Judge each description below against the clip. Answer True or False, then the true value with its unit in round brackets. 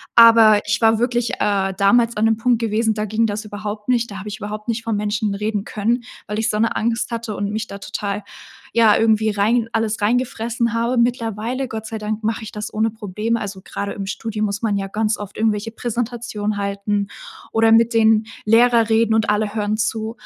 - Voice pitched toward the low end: False (220 Hz)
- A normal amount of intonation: False (1.7 semitones)